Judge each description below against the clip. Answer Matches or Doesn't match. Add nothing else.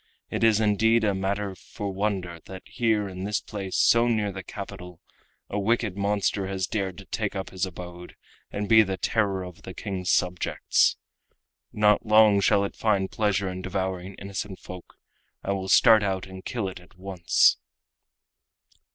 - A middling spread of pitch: Doesn't match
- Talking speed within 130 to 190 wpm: Matches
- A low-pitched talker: Matches